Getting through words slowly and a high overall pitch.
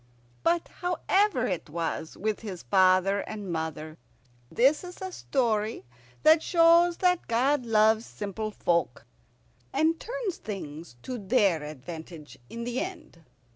Yes: slow, 130 wpm; high, 220 Hz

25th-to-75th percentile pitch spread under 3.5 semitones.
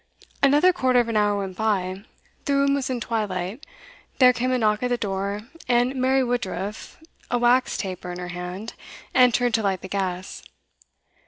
No: average, 4.7 semitones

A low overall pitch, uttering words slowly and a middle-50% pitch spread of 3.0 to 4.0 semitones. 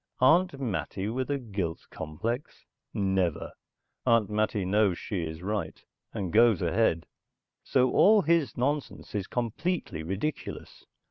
No: low, 110 Hz; slow, 125 wpm; wide, 5.6 semitones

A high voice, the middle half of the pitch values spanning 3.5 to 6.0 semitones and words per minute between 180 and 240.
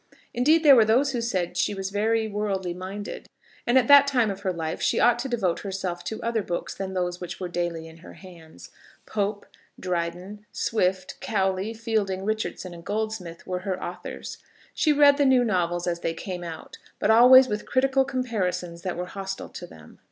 Yes: high, 195 Hz; average, 4.3 semitones; average, 195 wpm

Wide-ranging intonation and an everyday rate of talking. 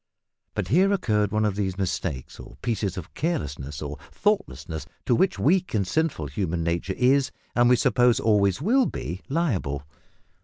Yes: wide, 8.3 semitones; average, 160 wpm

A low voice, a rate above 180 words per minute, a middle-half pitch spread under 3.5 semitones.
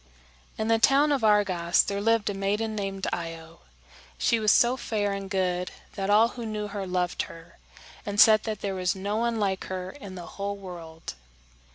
No: high, 200 Hz; average, 190 wpm; average, 2.8 semitones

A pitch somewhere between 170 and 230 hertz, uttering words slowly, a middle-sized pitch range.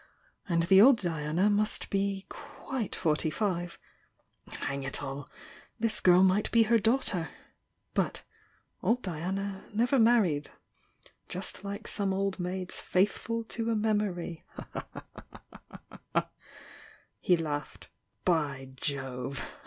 Yes: high, 190 Hz; slow, 125 wpm; average, 4.8 semitones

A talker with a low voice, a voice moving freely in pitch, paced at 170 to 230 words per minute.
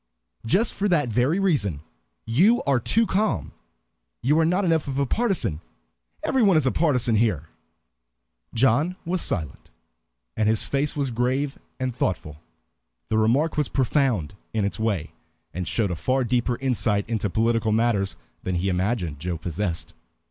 No: low, 120 Hz; wide, 6.5 semitones; average, 155 wpm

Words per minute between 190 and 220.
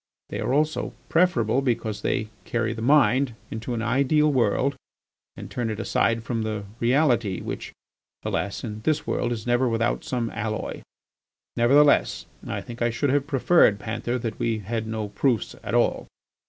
No: average, 165 wpm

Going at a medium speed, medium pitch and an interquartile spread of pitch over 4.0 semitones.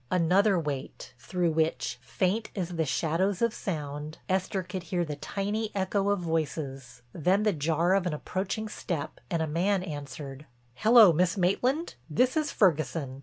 Yes: average, 160 wpm; medium, 175 Hz; average, 4.5 semitones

